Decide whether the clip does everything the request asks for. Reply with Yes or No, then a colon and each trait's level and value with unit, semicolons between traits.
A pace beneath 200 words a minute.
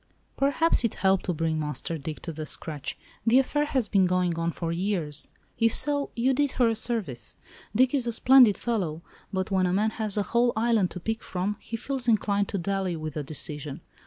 No: fast, 205 wpm